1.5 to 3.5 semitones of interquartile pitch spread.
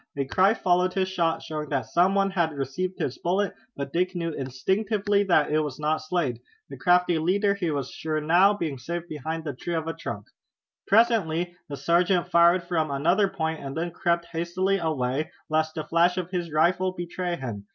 Yes: average, 3.1 semitones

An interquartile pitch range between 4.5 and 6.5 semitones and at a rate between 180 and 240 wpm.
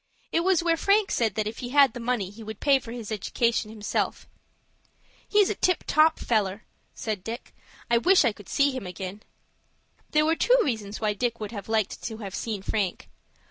Yes: average, 5.2 semitones; average, 195 wpm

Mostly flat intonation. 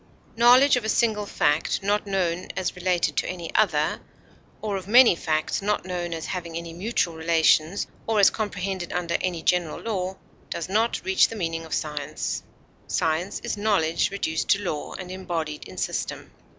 No: average, 3.8 semitones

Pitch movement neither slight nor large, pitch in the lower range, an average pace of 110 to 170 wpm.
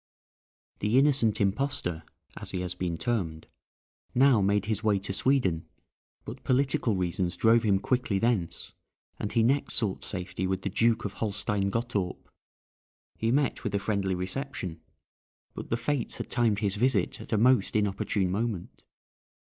Yes: average, 3.9 semitones; low, 105 Hz; average, 155 wpm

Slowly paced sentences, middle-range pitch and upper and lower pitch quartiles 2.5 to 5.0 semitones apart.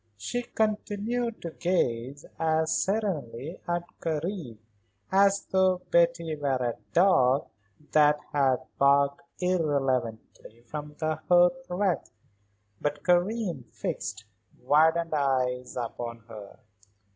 No: slow, 100 wpm; medium, 155 Hz; wide, 5.6 semitones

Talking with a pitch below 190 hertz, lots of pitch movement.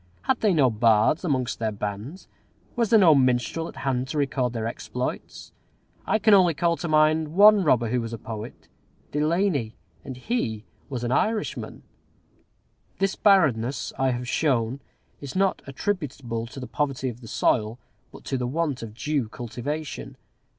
Yes: low, 135 Hz; wide, 5.8 semitones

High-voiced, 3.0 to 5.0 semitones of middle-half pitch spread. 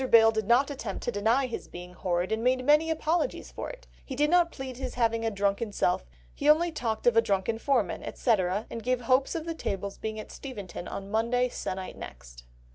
Yes: high, 230 Hz; average, 4.6 semitones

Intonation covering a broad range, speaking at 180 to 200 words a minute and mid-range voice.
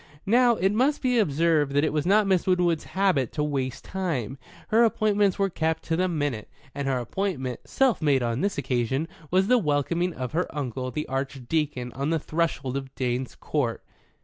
Yes: wide, 6.2 semitones; average, 185 wpm; medium, 155 Hz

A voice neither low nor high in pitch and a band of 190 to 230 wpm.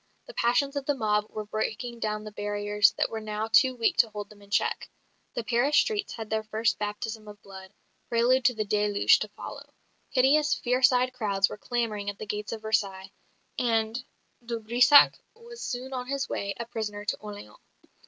No: high, 220 Hz; average, 195 wpm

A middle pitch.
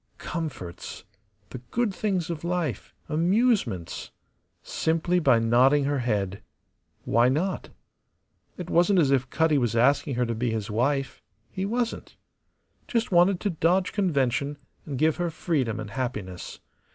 Yes: medium, 145 Hz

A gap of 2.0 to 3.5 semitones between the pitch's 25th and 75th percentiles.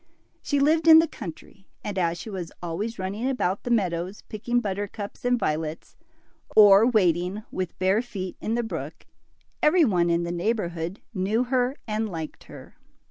No: average, 5.1 semitones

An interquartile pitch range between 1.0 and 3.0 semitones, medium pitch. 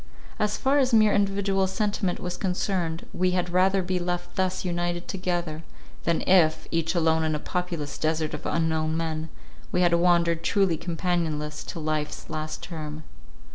Yes: narrow, 2.5 semitones; medium, 175 Hz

